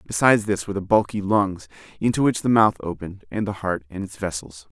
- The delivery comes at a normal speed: No, fast, 215 wpm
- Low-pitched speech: Yes, low, 100 Hz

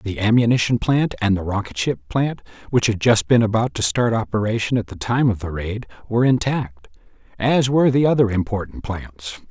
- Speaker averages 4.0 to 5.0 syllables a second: No, 5.3 syllables/s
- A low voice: Yes, low, 110 Hz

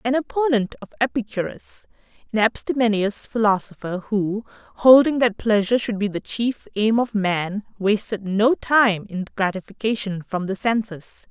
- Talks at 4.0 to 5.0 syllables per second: Yes, 4.6 syllables/s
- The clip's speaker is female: Yes, female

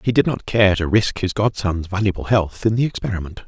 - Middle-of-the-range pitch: No, low, 100 Hz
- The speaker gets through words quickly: Yes, fast, 225 wpm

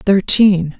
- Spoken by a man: No, female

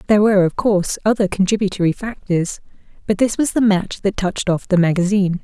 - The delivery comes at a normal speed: Yes, average, 190 wpm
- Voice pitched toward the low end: No, high, 195 Hz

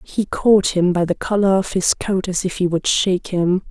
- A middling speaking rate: No, fast, 245 wpm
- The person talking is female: Yes, female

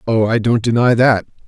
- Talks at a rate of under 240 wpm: Yes, fast, 205 wpm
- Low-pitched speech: Yes, low, 115 Hz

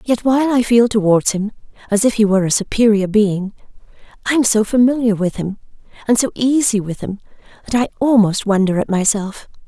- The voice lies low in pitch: No, high, 215 Hz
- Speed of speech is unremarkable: Yes, average, 185 wpm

